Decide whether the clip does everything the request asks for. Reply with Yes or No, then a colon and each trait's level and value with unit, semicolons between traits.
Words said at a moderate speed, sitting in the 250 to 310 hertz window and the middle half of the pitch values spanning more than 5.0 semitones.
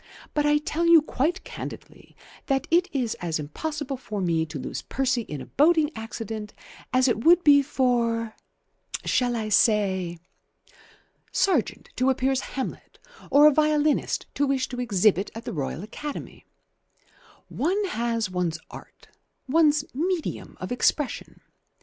Yes: average, 145 wpm; very high, 255 Hz; wide, 5.5 semitones